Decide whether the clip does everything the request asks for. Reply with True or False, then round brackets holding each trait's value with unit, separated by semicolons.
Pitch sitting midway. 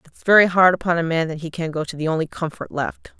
True (165 Hz)